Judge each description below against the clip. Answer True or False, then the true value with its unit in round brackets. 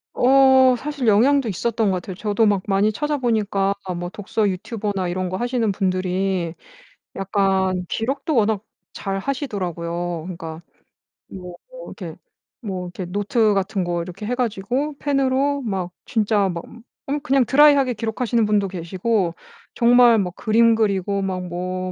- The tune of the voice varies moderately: True (4.6 semitones)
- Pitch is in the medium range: False (205 Hz)